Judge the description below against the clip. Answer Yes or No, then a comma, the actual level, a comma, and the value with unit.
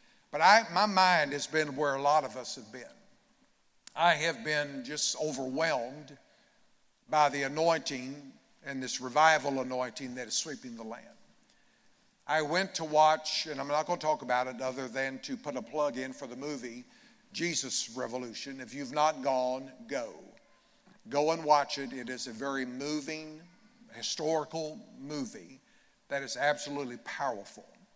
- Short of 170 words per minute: Yes, average, 160 wpm